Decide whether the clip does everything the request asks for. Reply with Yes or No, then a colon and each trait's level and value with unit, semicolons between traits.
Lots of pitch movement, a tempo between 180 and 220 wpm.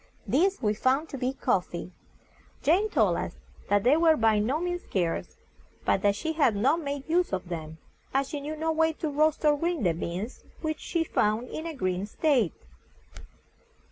Yes: wide, 7.3 semitones; average, 190 wpm